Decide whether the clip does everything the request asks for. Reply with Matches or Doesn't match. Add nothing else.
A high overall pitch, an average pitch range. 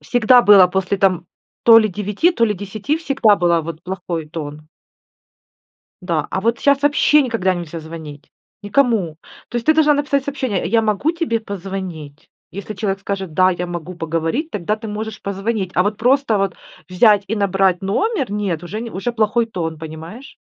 Matches